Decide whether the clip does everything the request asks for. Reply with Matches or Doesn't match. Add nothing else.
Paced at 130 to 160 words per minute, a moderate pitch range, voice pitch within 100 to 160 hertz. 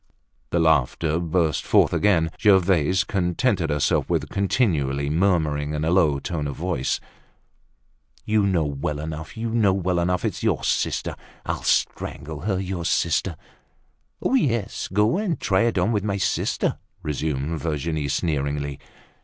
Doesn't match